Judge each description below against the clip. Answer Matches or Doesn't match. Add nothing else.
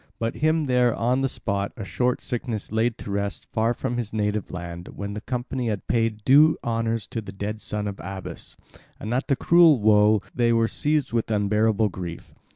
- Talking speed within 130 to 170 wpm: Doesn't match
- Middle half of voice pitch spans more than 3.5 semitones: Doesn't match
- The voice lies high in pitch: Doesn't match